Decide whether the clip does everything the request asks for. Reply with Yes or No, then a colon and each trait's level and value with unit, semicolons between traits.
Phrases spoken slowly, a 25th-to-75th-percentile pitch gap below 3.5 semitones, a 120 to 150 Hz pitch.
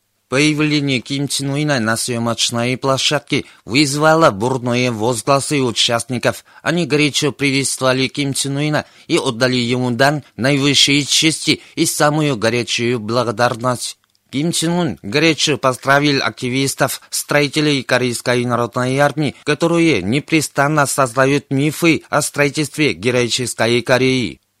Yes: slow, 105 wpm; average, 2.9 semitones; low, 135 Hz